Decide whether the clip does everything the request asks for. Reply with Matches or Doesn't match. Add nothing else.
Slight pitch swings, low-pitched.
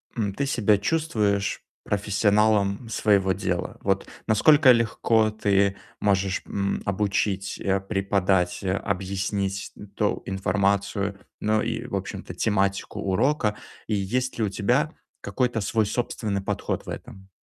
Matches